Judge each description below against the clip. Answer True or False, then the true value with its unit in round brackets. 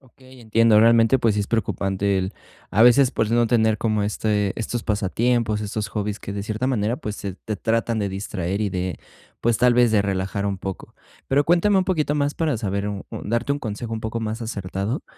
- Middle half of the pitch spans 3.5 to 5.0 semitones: False (2.9 semitones)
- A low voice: True (110 Hz)